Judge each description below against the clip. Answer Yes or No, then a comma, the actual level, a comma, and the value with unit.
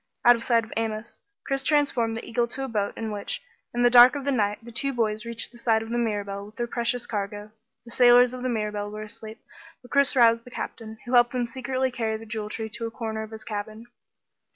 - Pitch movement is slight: Yes, narrow, 2.0 semitones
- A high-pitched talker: Yes, high, 230 Hz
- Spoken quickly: Yes, fast, 245 wpm